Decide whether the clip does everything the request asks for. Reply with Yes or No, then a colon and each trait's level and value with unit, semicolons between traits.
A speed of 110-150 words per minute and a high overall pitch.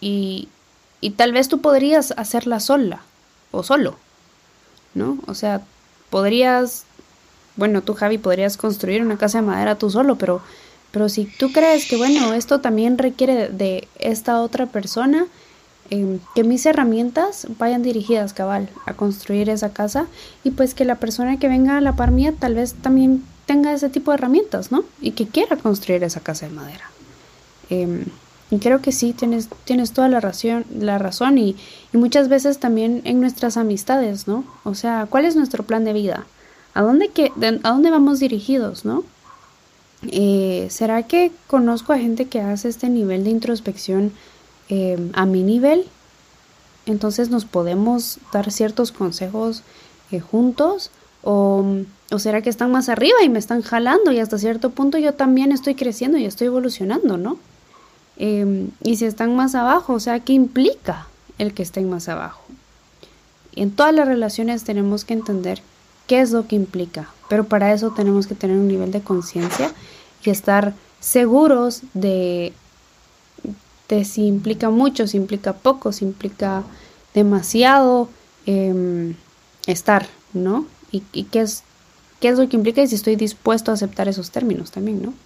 No: average, 165 wpm; high, 225 Hz